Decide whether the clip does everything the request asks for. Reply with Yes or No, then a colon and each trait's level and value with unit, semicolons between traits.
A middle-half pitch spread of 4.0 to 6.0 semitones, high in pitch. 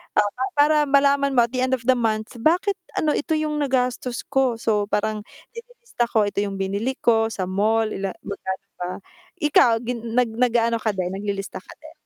Yes: average, 4.3 semitones; high, 235 Hz